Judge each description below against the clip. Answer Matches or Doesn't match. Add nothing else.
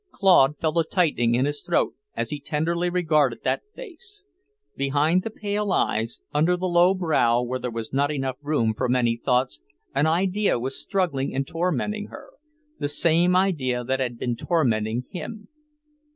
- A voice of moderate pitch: Matches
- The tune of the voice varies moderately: Doesn't match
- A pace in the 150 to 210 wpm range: Matches